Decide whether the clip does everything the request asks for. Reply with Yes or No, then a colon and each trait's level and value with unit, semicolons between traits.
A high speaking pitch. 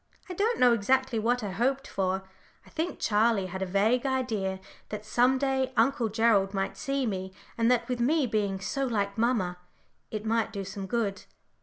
Yes: high, 225 Hz